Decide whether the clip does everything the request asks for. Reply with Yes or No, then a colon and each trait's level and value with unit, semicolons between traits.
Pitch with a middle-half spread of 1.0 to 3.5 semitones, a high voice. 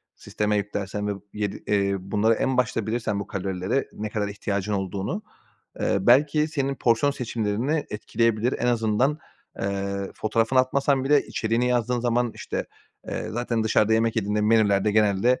No: average, 3.2 semitones; low, 110 Hz